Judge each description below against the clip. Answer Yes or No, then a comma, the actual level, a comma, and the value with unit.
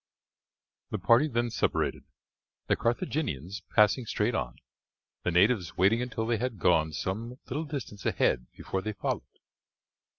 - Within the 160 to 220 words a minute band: No, slow, 135 wpm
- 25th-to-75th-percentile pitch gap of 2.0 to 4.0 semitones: No, average, 4.7 semitones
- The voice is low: Yes, low, 110 Hz